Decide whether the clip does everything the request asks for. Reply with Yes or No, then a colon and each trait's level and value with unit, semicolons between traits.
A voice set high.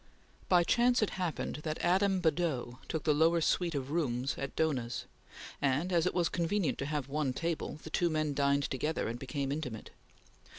No: medium, 155 Hz